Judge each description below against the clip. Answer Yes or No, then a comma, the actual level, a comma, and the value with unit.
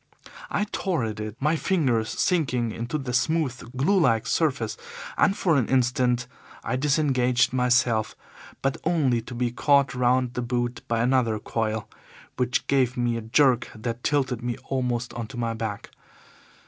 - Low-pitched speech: Yes, low, 125 Hz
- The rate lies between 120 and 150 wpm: No, average, 160 wpm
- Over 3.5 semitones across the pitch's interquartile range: No, narrow, 2.6 semitones